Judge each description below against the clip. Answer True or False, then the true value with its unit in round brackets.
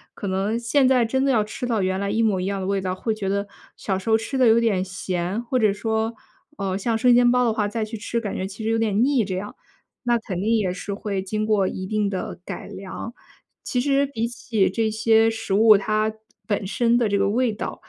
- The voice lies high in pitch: True (215 Hz)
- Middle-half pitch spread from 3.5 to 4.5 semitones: False (2.8 semitones)